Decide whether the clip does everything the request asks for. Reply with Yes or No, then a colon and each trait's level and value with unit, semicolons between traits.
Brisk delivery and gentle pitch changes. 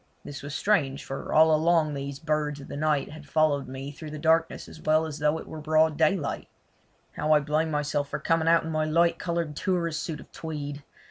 Yes: fast, 215 wpm; narrow, 1.7 semitones